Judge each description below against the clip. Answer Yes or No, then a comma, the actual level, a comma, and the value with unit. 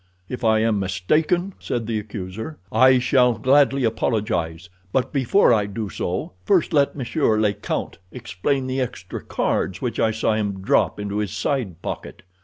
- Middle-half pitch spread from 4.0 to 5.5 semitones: Yes, average, 4.3 semitones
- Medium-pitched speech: No, low, 110 Hz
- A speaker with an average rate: Yes, average, 165 wpm